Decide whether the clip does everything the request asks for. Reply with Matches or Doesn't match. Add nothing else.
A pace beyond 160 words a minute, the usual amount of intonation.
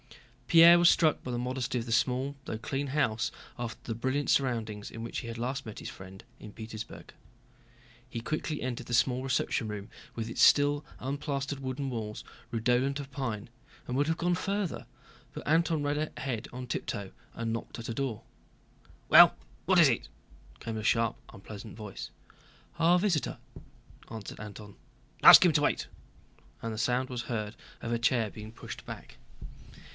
Matches